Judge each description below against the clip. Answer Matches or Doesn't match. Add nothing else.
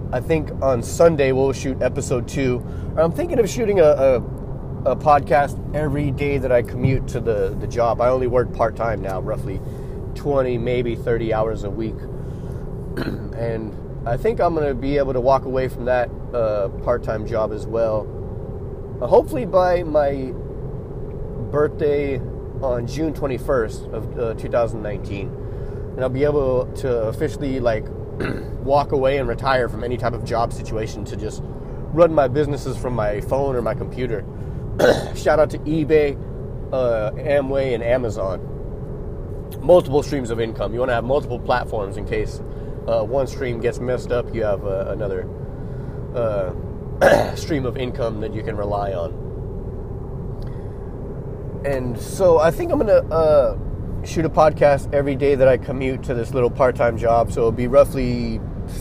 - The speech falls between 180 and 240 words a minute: Doesn't match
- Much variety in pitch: Doesn't match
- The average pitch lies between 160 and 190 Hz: Doesn't match